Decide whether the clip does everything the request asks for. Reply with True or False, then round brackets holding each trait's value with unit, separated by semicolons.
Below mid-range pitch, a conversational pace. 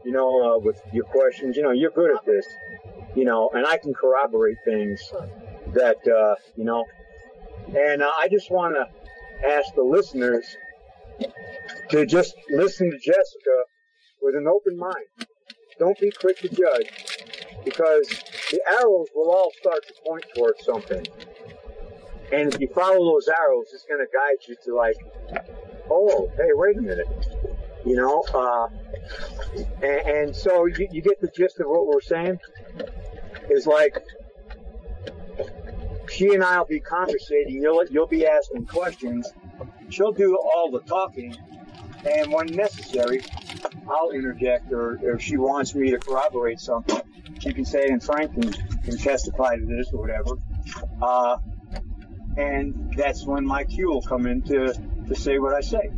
False (160 Hz; 160 wpm)